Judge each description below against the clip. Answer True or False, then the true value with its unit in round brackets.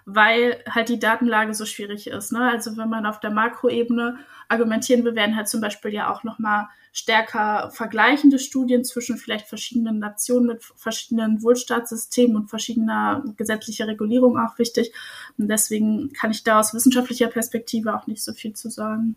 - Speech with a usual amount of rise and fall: False (1.9 semitones)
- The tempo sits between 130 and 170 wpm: True (165 wpm)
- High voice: True (225 Hz)